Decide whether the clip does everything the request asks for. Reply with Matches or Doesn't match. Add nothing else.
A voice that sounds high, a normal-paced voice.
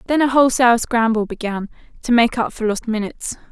Matches